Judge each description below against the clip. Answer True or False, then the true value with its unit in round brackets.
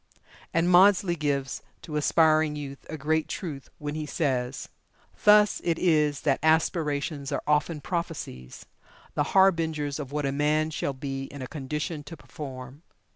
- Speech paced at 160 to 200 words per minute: False (150 wpm)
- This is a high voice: False (150 Hz)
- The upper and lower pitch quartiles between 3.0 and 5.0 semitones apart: False (2.5 semitones)